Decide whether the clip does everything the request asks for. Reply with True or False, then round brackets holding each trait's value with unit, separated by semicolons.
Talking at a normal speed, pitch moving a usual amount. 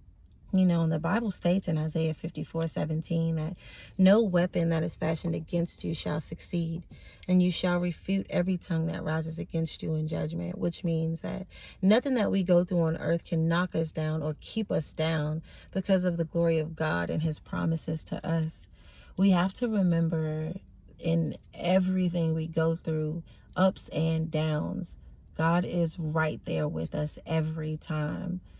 False (170 wpm; 1.9 semitones)